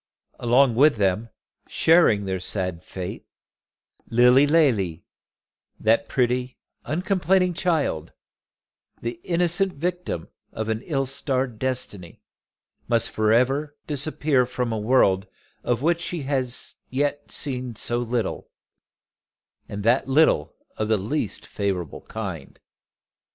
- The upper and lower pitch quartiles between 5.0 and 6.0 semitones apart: Yes, wide, 5.4 semitones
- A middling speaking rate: No, slow, 115 wpm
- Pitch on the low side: Yes, low, 125 Hz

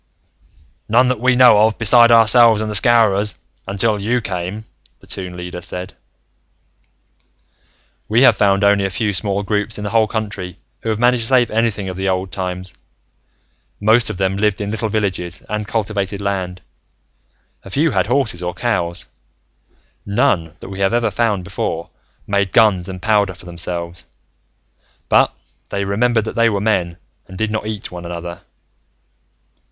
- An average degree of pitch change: Yes, average, 3.2 semitones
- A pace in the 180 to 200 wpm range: No, average, 165 wpm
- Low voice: Yes, low, 100 Hz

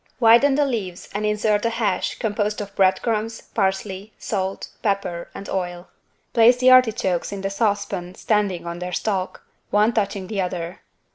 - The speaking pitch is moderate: No, high, 200 Hz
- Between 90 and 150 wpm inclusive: No, average, 160 wpm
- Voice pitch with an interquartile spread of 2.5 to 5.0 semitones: Yes, average, 2.9 semitones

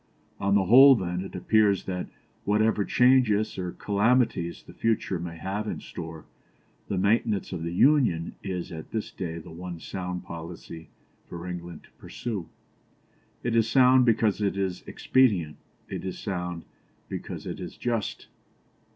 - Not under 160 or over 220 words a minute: No, average, 150 wpm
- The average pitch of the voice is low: Yes, very low, 95 Hz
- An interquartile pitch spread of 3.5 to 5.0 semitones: Yes, average, 4.2 semitones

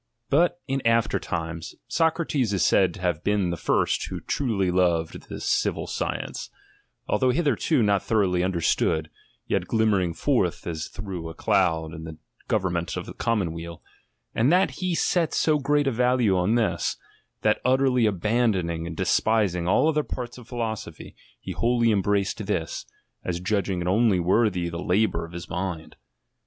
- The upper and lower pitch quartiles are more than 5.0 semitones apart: Yes, wide, 5.6 semitones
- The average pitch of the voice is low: Yes, low, 100 Hz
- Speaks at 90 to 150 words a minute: No, average, 165 wpm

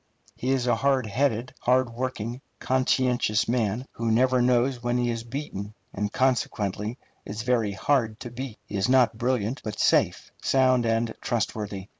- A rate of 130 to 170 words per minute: Yes, average, 160 wpm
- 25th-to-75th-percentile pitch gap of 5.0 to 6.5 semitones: No, average, 2.8 semitones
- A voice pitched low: Yes, low, 120 Hz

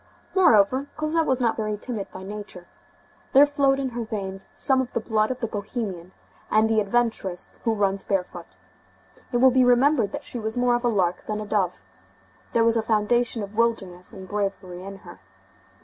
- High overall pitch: Yes, high, 220 Hz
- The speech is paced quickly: No, average, 190 wpm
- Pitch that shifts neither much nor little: Yes, average, 3.7 semitones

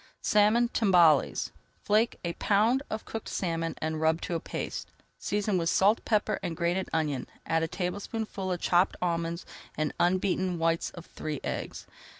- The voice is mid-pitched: Yes, medium, 180 Hz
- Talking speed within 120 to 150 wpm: No, average, 170 wpm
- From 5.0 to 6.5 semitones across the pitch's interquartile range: No, average, 3.8 semitones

